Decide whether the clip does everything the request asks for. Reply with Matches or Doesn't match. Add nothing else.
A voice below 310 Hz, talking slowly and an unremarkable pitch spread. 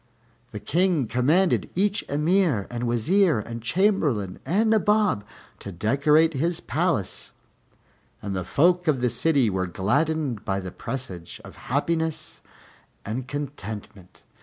Doesn't match